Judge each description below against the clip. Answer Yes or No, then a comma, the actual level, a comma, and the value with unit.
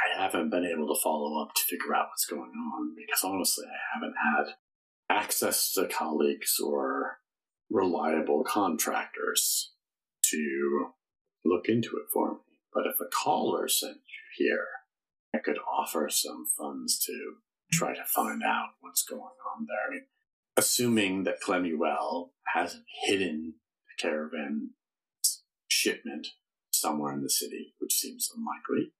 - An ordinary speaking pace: Yes, average, 145 wpm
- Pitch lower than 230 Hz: No, very high, 265 Hz